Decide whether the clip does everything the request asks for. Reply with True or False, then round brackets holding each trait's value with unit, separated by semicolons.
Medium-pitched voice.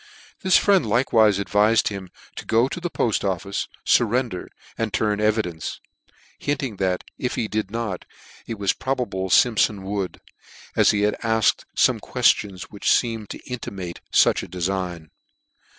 False (105 Hz)